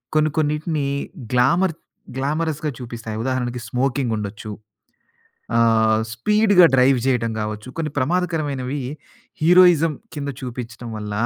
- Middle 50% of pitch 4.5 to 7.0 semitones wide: Yes, average, 4.9 semitones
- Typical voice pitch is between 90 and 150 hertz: Yes, low, 135 Hz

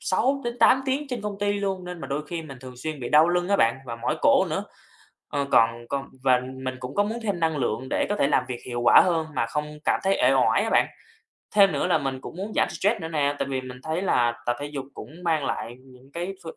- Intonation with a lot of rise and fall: Yes, wide, 6.8 semitones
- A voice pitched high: No, medium, 150 Hz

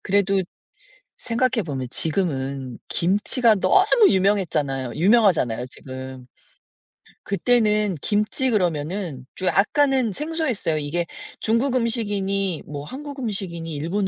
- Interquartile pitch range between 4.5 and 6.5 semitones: No, wide, 7.2 semitones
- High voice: Yes, high, 195 Hz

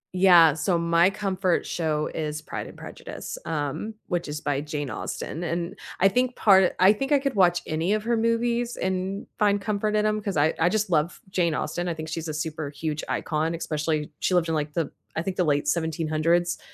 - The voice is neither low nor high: Yes, medium, 170 Hz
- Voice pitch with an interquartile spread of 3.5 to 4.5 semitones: Yes, average, 4.0 semitones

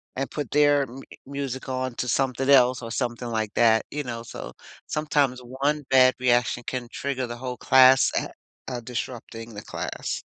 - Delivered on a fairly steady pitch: Yes, narrow, 2.1 semitones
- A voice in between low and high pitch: No, low, 130 Hz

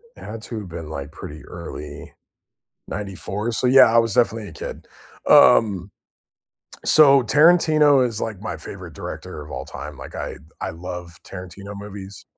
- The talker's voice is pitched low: Yes, low, 100 Hz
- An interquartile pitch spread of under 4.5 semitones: No, average, 5.3 semitones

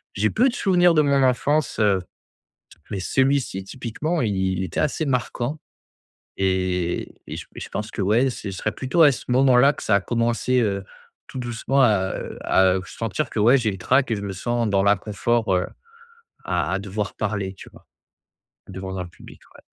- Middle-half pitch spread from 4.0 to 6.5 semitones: Yes, average, 5.3 semitones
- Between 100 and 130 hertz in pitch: Yes, low, 110 Hz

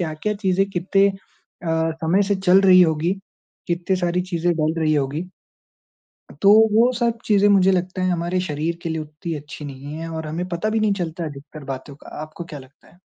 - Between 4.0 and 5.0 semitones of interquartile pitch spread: No, average, 3.3 semitones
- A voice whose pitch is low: No, medium, 170 Hz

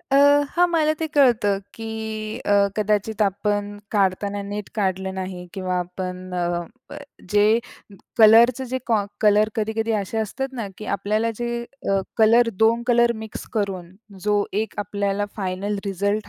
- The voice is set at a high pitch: Yes, high, 205 Hz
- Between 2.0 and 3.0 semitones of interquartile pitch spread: Yes, narrow, 2.4 semitones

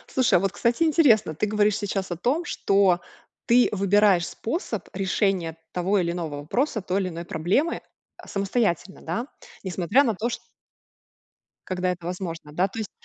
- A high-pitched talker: Yes, high, 195 Hz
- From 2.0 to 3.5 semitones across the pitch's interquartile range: No, average, 4.1 semitones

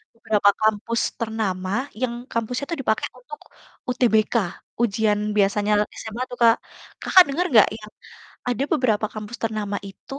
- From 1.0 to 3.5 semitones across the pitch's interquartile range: Yes, average, 2.8 semitones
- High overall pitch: Yes, high, 220 Hz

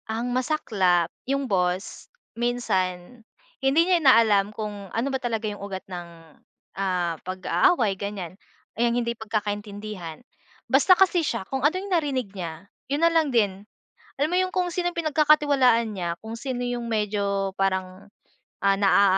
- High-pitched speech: Yes, high, 225 Hz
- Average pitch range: No, wide, 5.7 semitones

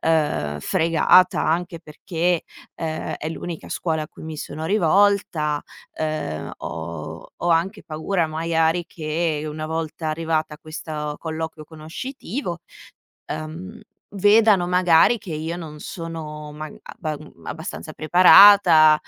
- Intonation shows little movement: Yes, narrow, 2.2 semitones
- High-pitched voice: No, medium, 160 Hz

